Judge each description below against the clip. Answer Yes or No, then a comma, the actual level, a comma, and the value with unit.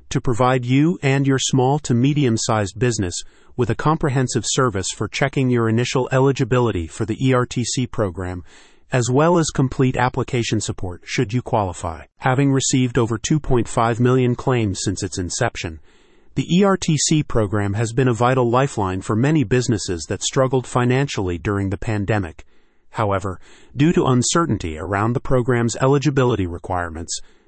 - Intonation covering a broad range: No, average, 4.4 semitones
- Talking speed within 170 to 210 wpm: No, average, 145 wpm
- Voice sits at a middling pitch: No, low, 125 Hz